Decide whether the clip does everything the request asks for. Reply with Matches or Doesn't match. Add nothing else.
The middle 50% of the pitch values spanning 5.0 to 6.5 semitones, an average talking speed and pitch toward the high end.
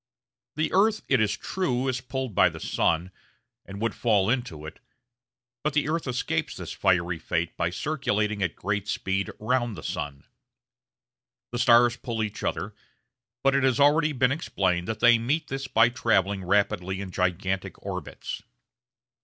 Doesn't match